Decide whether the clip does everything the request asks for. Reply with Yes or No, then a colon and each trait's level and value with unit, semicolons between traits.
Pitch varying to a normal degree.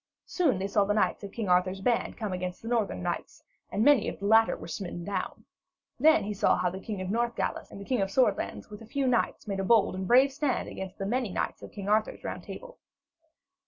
Yes: average, 3.8 semitones